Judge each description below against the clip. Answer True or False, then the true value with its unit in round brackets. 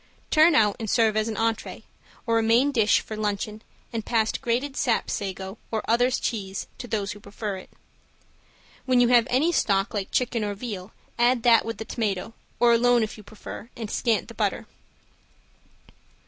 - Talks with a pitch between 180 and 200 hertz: False (225 Hz)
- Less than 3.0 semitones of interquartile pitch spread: True (2.6 semitones)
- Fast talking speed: False (180 wpm)